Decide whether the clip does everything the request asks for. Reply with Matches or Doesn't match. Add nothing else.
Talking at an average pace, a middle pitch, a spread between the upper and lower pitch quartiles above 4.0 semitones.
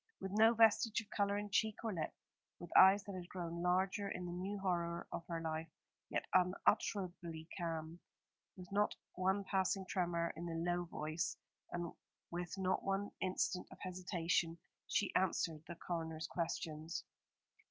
Doesn't match